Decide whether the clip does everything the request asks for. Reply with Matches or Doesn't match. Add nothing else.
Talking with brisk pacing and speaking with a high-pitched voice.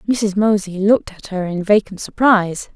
Doesn't match